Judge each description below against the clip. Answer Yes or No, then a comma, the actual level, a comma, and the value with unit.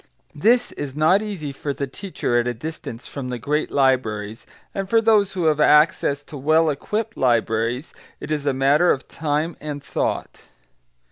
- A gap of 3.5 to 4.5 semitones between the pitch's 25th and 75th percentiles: Yes, average, 3.9 semitones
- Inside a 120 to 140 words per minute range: No, average, 175 wpm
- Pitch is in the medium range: Yes, medium, 145 Hz